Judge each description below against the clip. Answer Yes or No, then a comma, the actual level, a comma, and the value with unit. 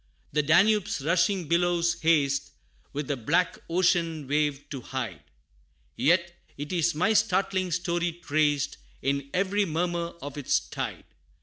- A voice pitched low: No, medium, 170 Hz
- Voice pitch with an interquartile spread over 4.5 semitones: No, average, 3.5 semitones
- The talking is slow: Yes, slow, 125 wpm